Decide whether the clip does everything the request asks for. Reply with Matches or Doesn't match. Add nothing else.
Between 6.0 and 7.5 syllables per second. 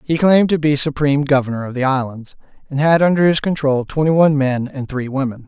Matches